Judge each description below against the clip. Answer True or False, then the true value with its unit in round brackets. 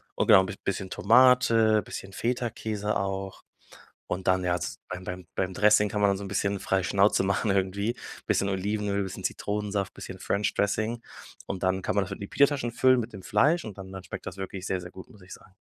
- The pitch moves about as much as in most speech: False (2.2 semitones)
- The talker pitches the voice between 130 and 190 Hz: False (100 Hz)